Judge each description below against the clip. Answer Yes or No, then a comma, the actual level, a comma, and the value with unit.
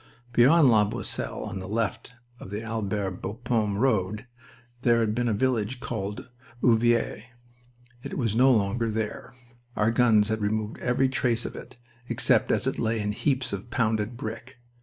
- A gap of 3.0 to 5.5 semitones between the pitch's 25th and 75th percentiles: No, narrow, 2.6 semitones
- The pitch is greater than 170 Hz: No, low, 115 Hz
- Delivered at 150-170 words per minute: Yes, average, 160 wpm